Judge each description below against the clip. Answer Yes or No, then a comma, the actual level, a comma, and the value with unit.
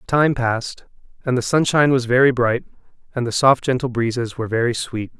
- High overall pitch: No, low, 125 Hz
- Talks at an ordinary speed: Yes, average, 185 wpm